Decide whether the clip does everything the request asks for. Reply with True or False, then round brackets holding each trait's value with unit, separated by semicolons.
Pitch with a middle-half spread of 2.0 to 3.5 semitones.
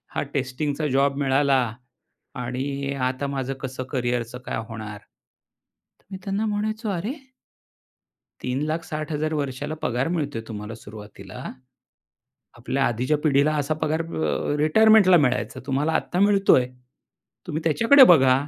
False (3.9 semitones)